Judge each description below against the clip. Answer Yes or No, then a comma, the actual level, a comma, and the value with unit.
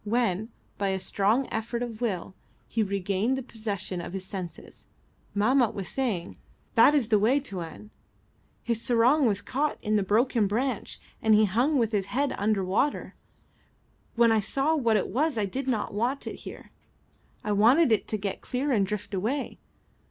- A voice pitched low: No, high, 220 Hz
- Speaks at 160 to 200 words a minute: Yes, average, 175 wpm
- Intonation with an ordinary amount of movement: Yes, average, 3.9 semitones